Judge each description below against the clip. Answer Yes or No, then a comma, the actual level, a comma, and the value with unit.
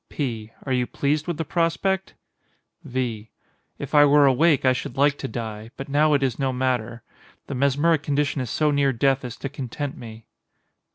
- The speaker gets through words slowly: No, average, 185 wpm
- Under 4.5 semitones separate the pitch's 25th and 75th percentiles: Yes, average, 3.0 semitones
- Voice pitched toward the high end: No, low, 135 Hz